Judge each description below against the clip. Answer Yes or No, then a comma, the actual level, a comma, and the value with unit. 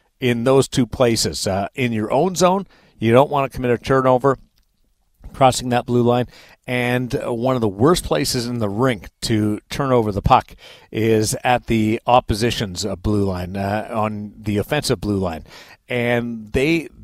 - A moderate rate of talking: Yes, average, 170 wpm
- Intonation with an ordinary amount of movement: Yes, average, 3.2 semitones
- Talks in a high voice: No, low, 120 Hz